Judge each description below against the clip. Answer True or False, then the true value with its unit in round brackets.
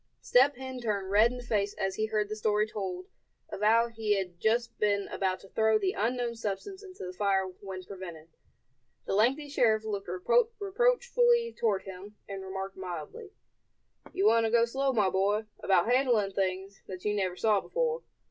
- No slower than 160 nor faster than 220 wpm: True (180 wpm)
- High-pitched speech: True (210 Hz)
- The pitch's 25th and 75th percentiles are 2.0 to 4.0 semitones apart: True (3.7 semitones)